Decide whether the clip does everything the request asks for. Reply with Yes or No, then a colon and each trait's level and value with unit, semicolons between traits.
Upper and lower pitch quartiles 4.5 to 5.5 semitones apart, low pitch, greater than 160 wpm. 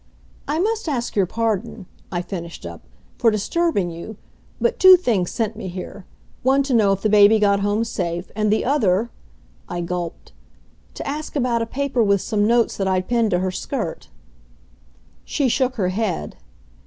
No: average, 4.9 semitones; high, 215 Hz; average, 175 wpm